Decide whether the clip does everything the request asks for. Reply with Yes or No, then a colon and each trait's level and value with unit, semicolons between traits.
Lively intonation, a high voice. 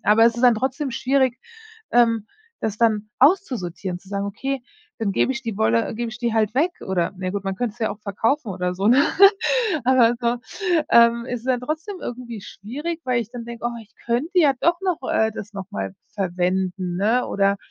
No: average, 4.1 semitones; high, 230 Hz